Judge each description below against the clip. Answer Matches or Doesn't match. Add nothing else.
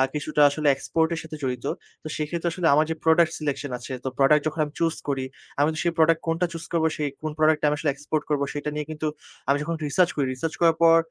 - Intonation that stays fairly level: Matches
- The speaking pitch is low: Doesn't match